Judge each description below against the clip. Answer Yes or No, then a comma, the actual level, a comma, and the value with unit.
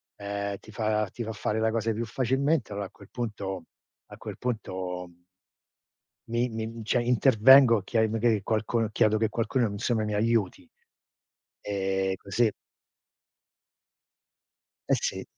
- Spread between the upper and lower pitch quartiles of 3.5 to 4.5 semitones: No, narrow, 2.5 semitones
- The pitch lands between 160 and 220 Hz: No, low, 110 Hz